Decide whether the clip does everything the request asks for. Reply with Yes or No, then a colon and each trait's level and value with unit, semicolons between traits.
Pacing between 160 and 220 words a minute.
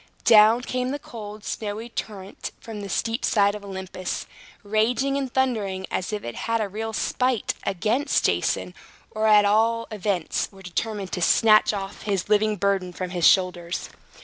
Yes: average, 165 wpm